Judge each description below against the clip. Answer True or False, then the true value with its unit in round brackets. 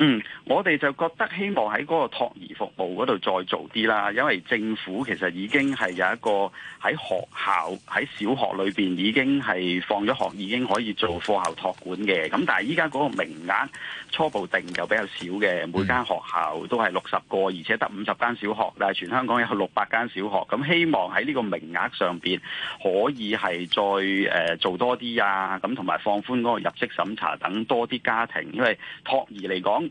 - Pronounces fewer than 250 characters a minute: False (290 characters per minute)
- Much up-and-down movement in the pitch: False (4.0 semitones)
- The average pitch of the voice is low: True (105 Hz)